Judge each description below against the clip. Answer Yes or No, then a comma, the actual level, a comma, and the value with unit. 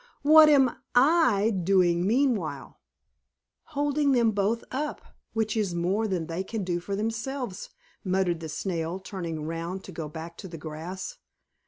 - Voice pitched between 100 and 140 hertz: No, high, 195 Hz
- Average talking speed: Yes, average, 150 wpm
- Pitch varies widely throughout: Yes, wide, 6.0 semitones